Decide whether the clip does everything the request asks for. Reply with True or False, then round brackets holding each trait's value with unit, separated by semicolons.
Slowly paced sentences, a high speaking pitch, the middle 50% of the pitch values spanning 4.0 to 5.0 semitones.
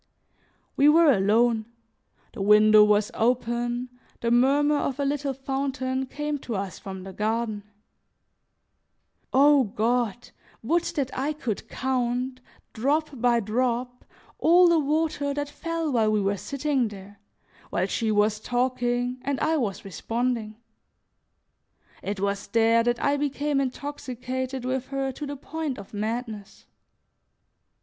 True (130 wpm; 250 Hz; 4.3 semitones)